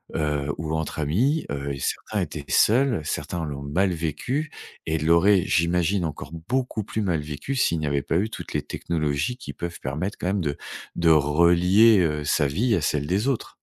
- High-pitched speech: No, very low, 85 Hz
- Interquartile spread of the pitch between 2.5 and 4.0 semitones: No, wide, 5.5 semitones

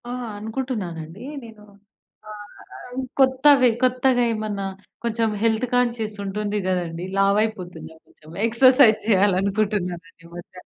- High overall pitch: Yes, high, 215 Hz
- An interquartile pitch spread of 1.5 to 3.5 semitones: No, average, 4.2 semitones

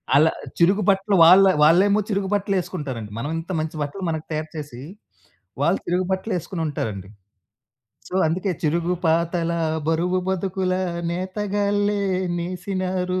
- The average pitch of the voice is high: No, medium, 180 Hz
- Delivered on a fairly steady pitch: No, average, 3.2 semitones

